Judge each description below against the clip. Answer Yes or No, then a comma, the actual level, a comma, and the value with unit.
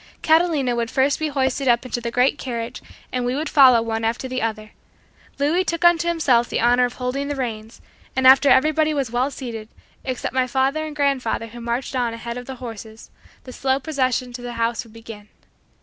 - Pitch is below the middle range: No, very high, 255 Hz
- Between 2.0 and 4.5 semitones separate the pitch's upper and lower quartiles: Yes, average, 2.9 semitones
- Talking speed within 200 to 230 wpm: Yes, fast, 205 wpm